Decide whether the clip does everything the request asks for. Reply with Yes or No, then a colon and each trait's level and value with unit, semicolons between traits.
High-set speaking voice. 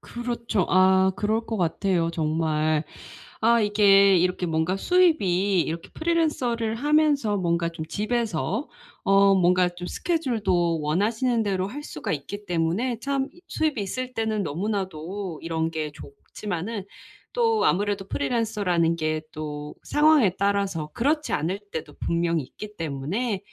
Yes: high, 195 Hz